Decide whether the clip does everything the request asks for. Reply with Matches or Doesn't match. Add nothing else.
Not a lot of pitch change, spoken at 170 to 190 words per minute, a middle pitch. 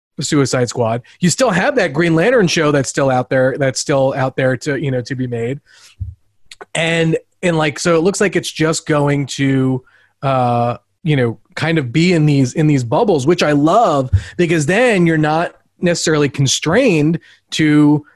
Doesn't match